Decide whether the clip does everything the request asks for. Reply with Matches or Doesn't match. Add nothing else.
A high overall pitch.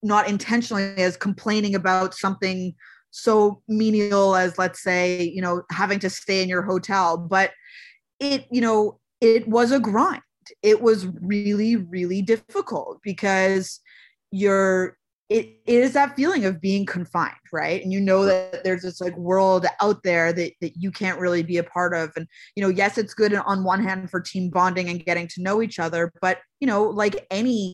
Matches